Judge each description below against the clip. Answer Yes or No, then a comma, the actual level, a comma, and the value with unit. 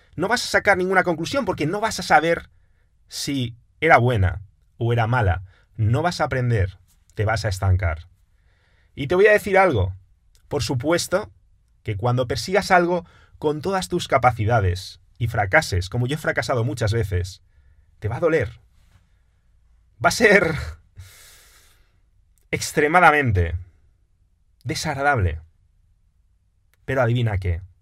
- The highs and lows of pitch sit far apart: Yes, wide, 8.0 semitones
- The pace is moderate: No, slow, 130 wpm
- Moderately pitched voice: No, low, 105 Hz